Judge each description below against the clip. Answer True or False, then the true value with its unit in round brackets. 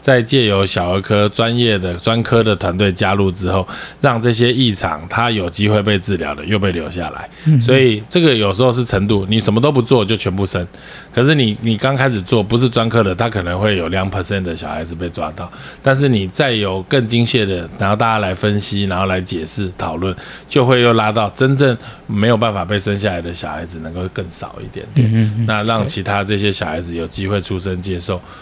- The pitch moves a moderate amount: True (3.8 semitones)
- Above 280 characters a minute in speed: True (325 characters per minute)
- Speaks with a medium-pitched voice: False (105 Hz)